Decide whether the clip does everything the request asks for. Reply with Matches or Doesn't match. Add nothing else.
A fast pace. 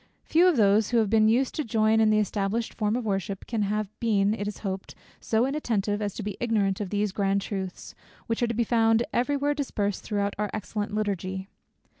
Matches